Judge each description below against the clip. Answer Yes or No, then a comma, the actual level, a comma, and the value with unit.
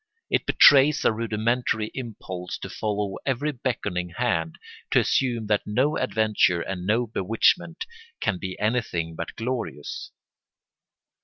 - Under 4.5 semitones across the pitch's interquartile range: No, average, 4.8 semitones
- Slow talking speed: Yes, slow, 125 wpm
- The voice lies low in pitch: Yes, low, 110 Hz